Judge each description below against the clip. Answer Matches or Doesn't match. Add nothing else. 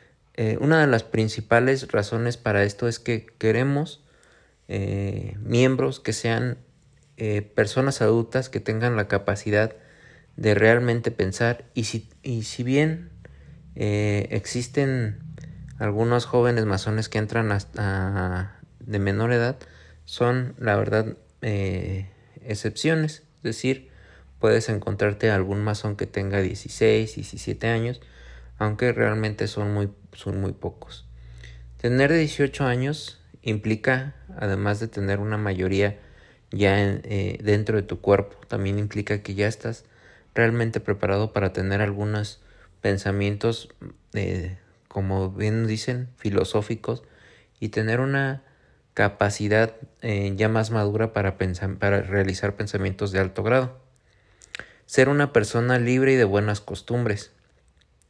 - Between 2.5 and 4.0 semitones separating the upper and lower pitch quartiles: Matches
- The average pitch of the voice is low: Matches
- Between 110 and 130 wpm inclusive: Matches